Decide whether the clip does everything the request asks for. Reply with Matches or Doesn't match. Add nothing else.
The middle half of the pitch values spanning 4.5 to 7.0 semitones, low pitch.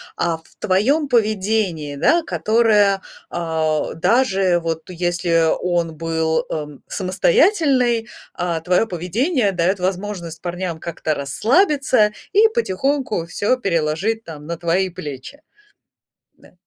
Doesn't match